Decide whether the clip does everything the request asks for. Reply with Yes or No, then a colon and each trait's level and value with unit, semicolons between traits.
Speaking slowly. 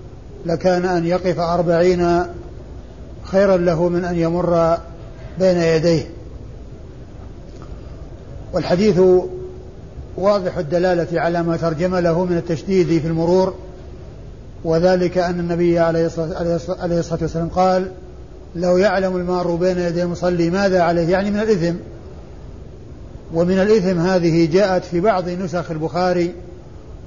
No: average, 105 wpm